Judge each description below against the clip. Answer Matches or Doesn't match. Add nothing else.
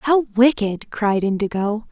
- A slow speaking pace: Matches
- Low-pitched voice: Doesn't match